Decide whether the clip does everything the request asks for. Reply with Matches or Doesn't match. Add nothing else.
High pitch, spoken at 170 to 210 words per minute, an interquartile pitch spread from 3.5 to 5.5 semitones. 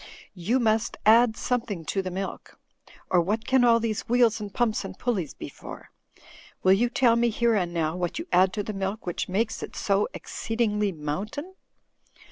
Matches